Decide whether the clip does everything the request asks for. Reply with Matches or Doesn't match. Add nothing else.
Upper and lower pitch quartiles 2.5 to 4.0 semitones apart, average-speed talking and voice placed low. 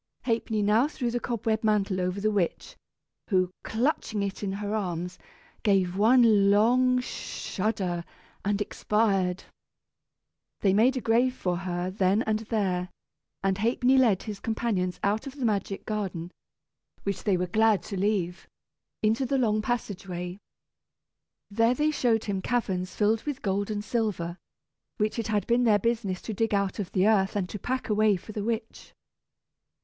Doesn't match